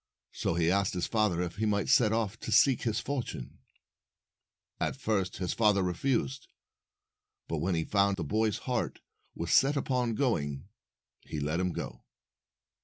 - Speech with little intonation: No, average, 4.6 semitones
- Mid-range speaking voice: No, low, 105 Hz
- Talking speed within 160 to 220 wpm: Yes, average, 165 wpm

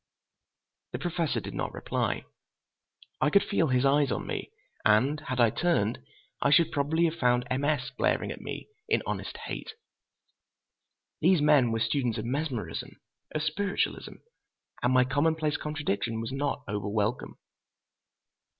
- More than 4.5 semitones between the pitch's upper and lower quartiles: No, average, 4.1 semitones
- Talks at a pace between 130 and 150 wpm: Yes, average, 145 wpm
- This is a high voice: No, medium, 140 Hz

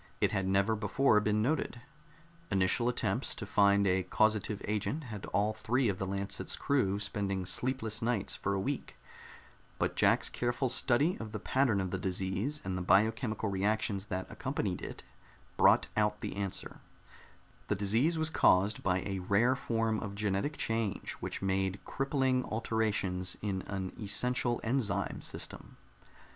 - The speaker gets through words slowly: No, average, 155 wpm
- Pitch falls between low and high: No, low, 105 Hz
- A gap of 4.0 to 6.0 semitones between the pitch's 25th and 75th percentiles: No, average, 3.6 semitones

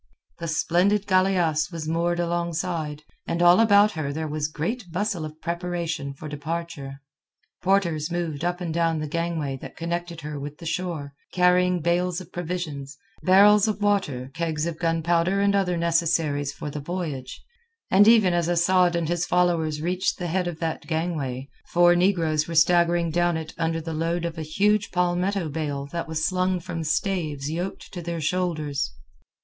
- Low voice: No, medium, 170 Hz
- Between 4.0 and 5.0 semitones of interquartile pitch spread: No, narrow, 2.4 semitones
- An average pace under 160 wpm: No, average, 170 wpm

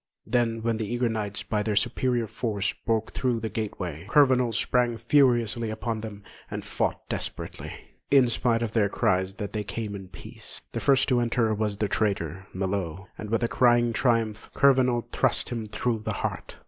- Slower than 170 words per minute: No, average, 185 wpm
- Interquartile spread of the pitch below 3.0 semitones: Yes, narrow, 2.6 semitones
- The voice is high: No, low, 115 Hz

